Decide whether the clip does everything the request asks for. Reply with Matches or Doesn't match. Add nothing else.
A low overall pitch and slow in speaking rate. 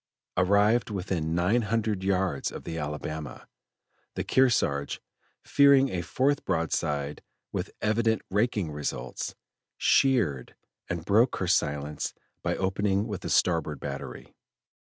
Matches